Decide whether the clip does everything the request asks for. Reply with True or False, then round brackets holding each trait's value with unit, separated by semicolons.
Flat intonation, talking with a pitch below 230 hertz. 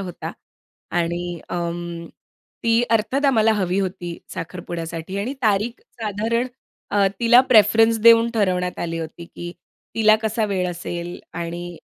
False (4.5 semitones; 190 Hz)